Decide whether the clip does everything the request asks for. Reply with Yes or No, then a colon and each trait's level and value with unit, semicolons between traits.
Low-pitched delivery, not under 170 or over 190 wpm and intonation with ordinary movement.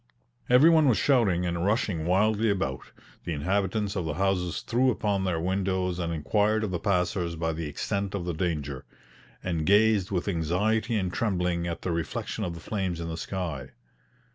Yes: very low, 90 Hz; average, 180 wpm; average, 3.4 semitones